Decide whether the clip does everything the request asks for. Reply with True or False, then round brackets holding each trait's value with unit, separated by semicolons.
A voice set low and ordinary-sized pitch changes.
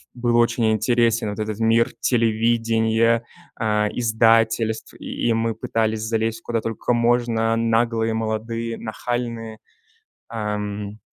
False (115 Hz; 1.0 semitones)